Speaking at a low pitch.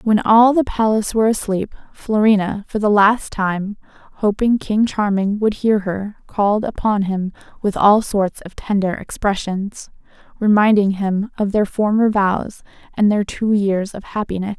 No: high, 205 Hz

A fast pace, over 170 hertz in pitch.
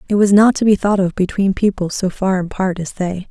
Yes: fast, 255 wpm; high, 190 Hz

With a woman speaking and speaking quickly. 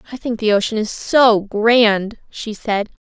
No: female; average, 175 wpm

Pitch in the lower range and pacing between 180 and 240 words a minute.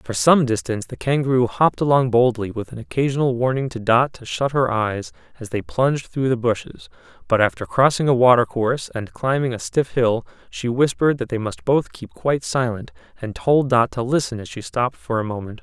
Yes: low, 120 Hz; fast, 205 wpm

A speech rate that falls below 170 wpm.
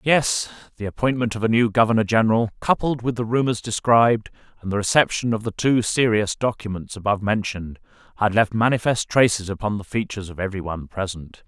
No: average, 180 wpm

